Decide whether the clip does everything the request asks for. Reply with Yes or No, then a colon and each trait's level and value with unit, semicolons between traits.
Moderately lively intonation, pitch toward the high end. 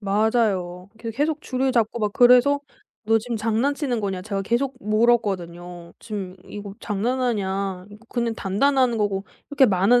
Yes: average, 3.9 semitones; high, 220 Hz